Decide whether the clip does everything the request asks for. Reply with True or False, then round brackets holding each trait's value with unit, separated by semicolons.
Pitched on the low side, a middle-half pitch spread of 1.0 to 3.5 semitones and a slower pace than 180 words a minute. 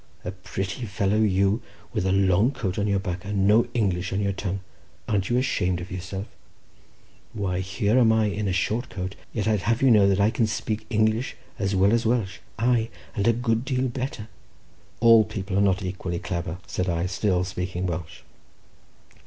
False (100 Hz; 3.1 semitones; 195 wpm)